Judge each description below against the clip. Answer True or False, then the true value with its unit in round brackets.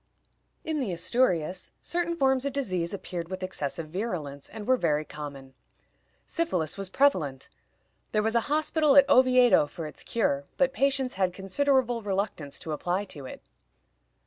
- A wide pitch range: True (8.3 semitones)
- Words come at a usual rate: True (150 wpm)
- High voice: True (195 Hz)